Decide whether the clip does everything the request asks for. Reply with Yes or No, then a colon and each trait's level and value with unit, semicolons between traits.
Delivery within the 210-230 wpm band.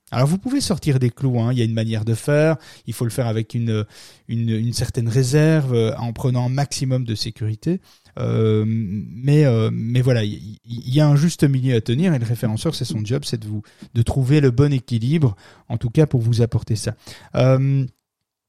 Yes: fast, 220 wpm